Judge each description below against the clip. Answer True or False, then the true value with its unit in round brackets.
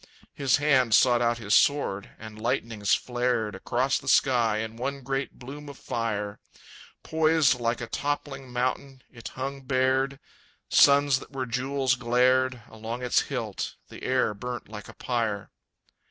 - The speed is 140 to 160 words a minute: True (150 wpm)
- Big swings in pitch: False (2.8 semitones)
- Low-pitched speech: True (125 Hz)